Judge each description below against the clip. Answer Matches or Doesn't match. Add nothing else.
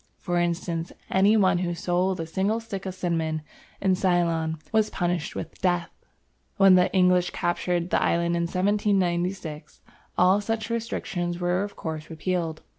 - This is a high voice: Doesn't match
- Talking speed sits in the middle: Matches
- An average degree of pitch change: Doesn't match